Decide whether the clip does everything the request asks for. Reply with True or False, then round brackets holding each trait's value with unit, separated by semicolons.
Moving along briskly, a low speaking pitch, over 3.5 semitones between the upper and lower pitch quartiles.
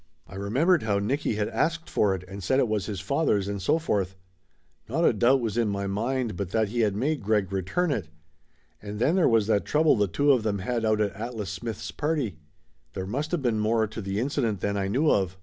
True (235 wpm; 110 Hz; 4.9 semitones)